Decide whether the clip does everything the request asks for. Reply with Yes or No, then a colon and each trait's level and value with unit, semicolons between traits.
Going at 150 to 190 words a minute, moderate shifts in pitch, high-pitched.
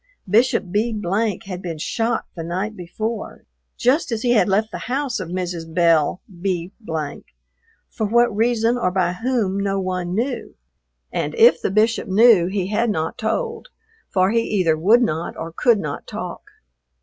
Yes: average, 160 wpm; average, 4.4 semitones; high, 205 Hz